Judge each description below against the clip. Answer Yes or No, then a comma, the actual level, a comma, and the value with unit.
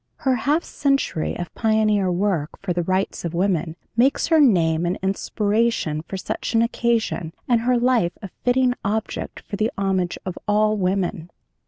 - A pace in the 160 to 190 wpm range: Yes, average, 165 wpm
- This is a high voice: Yes, high, 205 Hz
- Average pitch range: Yes, average, 4.7 semitones